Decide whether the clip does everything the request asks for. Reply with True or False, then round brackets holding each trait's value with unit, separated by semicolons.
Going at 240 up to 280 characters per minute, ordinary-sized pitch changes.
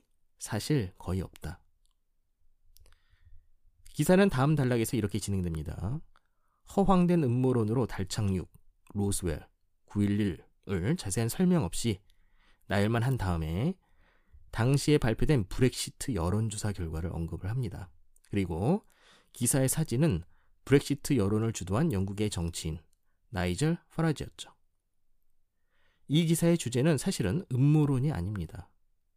False (260 characters per minute; 7.7 semitones)